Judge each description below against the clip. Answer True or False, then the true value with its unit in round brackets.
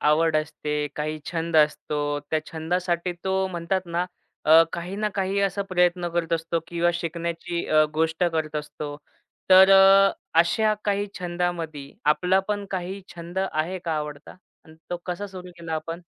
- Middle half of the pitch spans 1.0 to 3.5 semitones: True (2.8 semitones)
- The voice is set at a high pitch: False (170 Hz)